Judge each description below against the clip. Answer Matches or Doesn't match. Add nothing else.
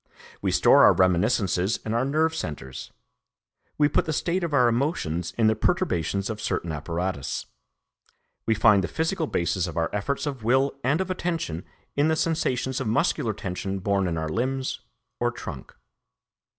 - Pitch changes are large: Matches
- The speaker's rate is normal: Matches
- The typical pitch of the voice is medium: Doesn't match